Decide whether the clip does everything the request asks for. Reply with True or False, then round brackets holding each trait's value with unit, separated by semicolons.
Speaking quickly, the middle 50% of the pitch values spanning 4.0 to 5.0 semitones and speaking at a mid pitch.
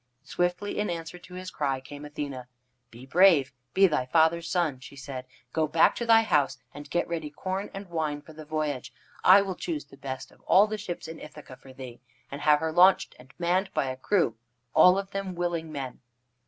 True (210 wpm; 4.6 semitones; 160 Hz)